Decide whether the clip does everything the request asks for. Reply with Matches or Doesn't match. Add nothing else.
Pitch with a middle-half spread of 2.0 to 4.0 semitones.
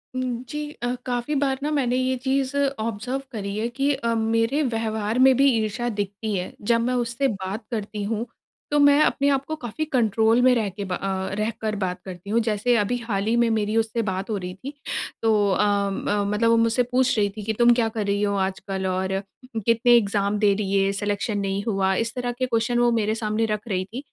Matches